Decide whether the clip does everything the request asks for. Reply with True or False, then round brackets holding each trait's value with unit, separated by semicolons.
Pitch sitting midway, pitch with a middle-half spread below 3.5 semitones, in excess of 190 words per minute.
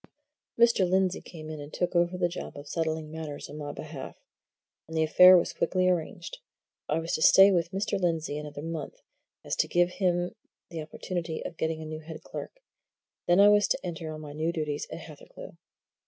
True (165 Hz; 2.6 semitones; 200 wpm)